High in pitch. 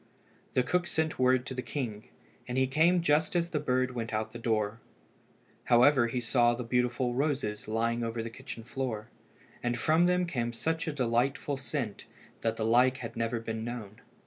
No: low, 125 Hz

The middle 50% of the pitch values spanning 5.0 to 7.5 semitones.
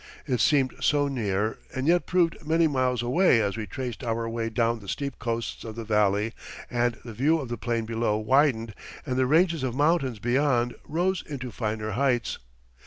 No: average, 3.9 semitones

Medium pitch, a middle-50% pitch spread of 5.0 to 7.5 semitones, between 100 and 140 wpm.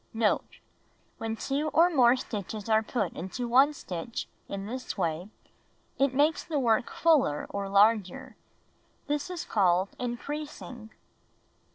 No: high, 235 Hz; wide, 5.4 semitones; slow, 135 wpm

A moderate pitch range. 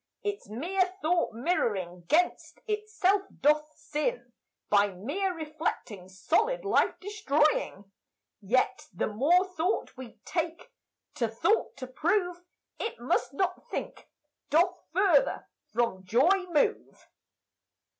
No: wide, 7.9 semitones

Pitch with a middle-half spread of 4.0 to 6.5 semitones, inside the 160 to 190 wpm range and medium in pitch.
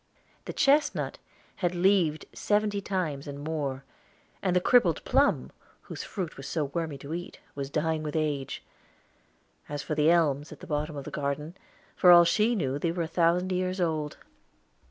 No: average, 3.6 semitones; average, 175 wpm; medium, 160 Hz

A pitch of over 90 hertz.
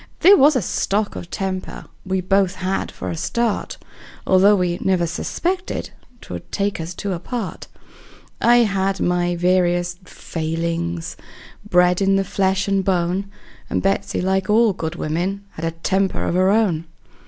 Yes: medium, 185 Hz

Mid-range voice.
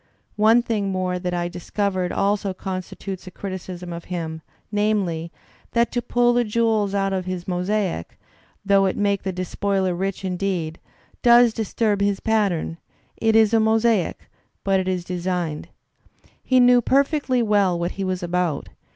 No: high, 195 Hz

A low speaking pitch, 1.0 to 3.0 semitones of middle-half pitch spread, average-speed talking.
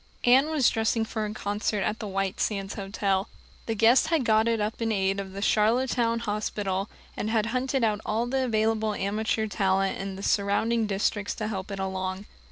No: high, 215 Hz; narrow, 2.5 semitones; average, 190 wpm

